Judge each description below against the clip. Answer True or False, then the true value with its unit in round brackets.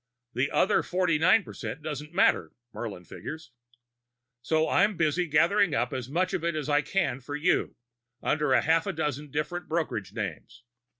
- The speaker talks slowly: False (165 wpm)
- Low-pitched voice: False (155 Hz)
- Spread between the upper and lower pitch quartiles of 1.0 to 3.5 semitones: False (4.3 semitones)